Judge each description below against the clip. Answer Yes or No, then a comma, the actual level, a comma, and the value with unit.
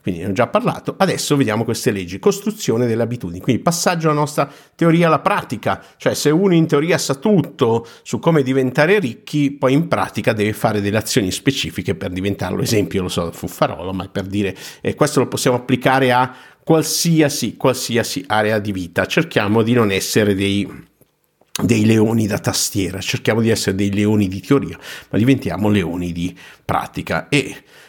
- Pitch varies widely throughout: Yes, wide, 6.5 semitones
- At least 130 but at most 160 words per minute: No, fast, 170 wpm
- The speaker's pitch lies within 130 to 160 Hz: No, low, 120 Hz